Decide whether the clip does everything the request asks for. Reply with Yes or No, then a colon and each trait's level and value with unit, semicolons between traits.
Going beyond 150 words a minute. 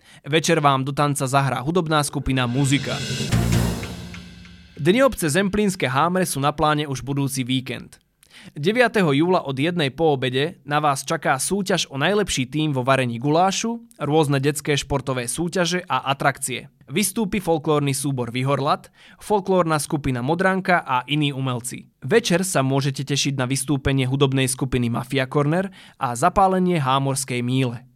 No: average, 135 wpm